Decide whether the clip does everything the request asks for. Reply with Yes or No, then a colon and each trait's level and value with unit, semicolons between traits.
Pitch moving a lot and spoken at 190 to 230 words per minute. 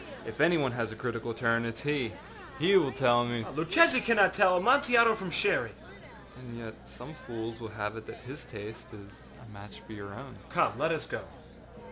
Yes: wide, 7.3 semitones; average, 200 wpm